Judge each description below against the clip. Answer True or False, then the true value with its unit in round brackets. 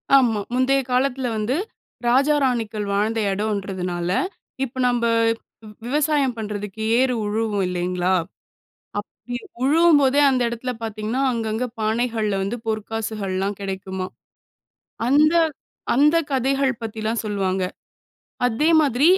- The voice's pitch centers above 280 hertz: False (225 Hz)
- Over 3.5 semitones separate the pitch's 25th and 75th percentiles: True (4.1 semitones)